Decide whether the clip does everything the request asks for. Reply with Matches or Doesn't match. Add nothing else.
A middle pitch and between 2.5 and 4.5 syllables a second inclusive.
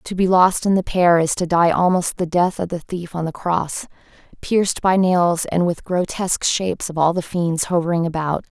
Doesn't match